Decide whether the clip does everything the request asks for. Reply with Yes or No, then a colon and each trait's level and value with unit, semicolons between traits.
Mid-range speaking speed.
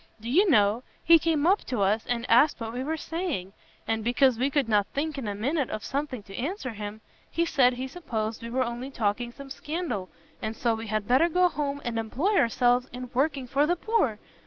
No: fast, 220 wpm